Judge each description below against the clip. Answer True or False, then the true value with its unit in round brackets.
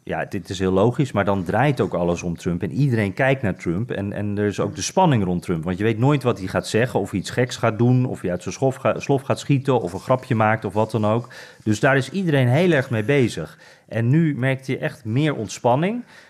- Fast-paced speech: True (260 wpm)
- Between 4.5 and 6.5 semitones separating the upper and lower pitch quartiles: True (5.0 semitones)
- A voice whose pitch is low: True (120 Hz)